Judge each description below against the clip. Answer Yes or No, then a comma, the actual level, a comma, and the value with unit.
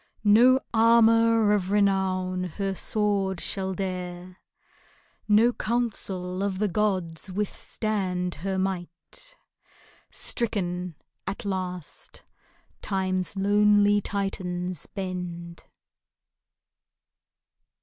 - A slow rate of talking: Yes, slow, 75 wpm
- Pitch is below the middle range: No, high, 195 Hz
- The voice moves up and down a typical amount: No, narrow, 2.3 semitones